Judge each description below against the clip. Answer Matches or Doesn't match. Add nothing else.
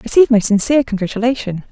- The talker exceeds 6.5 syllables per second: Matches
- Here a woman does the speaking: Matches